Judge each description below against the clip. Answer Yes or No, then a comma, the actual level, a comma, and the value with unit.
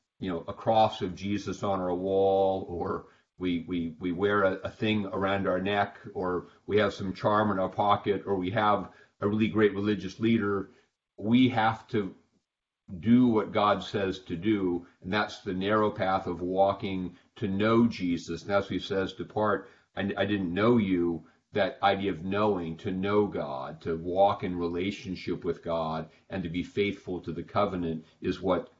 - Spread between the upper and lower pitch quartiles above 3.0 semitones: No, narrow, 2.5 semitones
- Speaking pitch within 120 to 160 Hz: No, low, 100 Hz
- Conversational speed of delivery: Yes, average, 180 wpm